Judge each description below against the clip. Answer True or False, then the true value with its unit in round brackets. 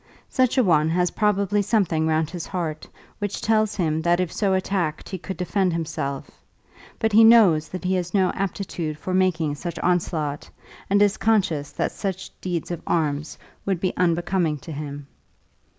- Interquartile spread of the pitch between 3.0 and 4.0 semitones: True (3.7 semitones)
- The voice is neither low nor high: True (180 Hz)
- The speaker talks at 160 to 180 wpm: True (170 wpm)